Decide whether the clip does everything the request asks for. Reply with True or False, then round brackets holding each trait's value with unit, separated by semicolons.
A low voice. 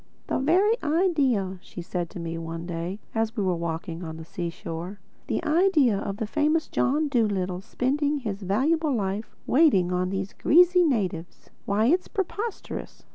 False (210 Hz)